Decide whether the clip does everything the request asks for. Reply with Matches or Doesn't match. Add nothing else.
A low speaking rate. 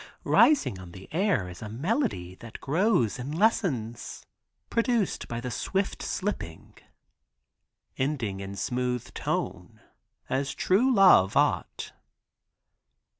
Matches